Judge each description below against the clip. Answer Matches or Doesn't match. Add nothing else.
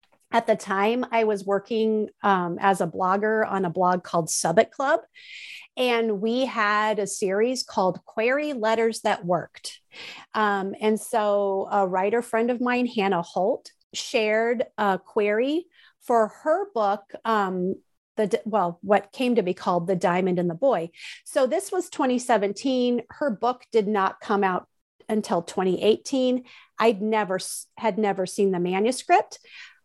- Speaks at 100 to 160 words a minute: Matches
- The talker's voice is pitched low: Doesn't match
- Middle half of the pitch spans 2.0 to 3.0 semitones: Doesn't match